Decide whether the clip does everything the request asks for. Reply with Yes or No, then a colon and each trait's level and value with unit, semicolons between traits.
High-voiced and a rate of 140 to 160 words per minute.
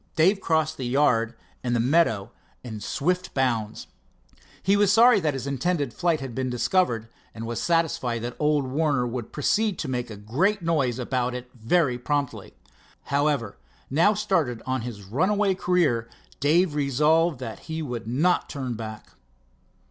No: medium, 140 Hz; average, 155 wpm